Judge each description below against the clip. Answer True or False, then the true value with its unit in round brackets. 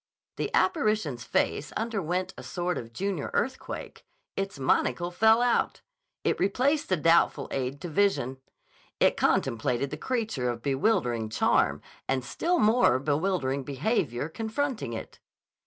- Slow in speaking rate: True (130 wpm)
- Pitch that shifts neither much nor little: False (8.7 semitones)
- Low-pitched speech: False (170 Hz)